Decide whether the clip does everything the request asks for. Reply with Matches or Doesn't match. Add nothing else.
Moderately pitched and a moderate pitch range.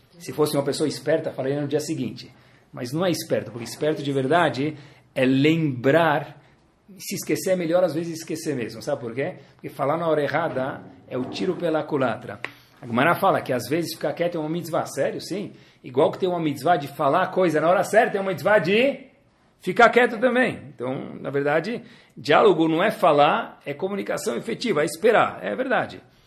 Matches